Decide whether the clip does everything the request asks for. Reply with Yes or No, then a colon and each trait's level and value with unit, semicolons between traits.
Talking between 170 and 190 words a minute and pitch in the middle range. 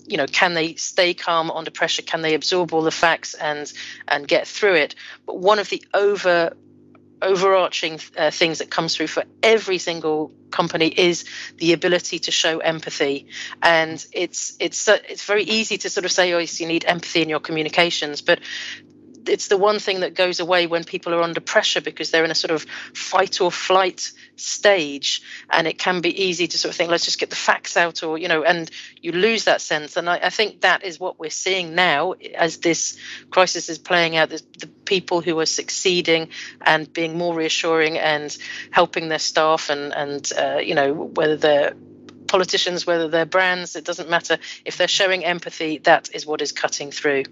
No: average, 200 wpm; medium, 170 Hz